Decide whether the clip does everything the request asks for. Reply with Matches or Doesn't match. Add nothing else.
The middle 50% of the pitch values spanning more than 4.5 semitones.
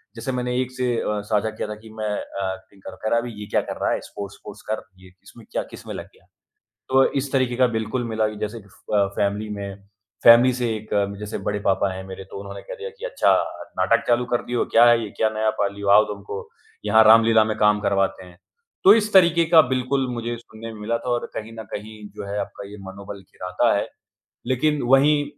Doesn't match